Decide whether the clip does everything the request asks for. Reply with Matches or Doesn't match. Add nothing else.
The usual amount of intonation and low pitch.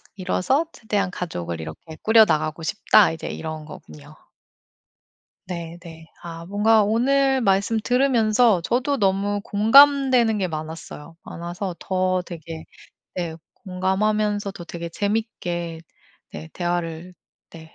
Doesn't match